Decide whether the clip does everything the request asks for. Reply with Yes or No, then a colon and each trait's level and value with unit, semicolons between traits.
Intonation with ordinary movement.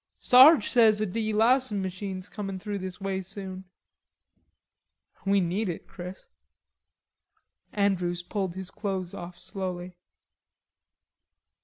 No: narrow, 2.3 semitones